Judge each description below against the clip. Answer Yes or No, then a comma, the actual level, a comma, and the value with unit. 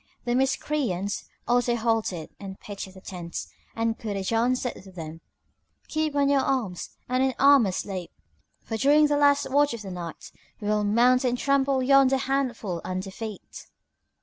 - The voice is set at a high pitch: Yes, high, 235 Hz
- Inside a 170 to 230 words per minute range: No, average, 160 wpm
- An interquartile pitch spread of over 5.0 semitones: Yes, wide, 5.6 semitones